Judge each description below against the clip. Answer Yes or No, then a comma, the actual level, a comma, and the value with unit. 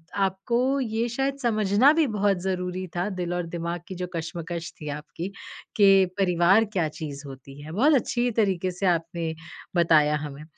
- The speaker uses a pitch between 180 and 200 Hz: Yes, medium, 185 Hz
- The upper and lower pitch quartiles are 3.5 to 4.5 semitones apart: Yes, average, 4.2 semitones